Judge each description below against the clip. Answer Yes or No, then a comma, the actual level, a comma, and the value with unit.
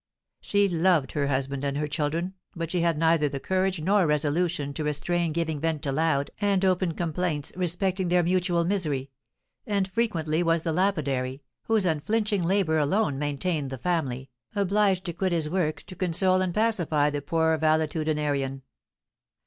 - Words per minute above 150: Yes, average, 160 wpm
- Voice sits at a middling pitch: Yes, medium, 165 Hz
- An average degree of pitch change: Yes, average, 3.9 semitones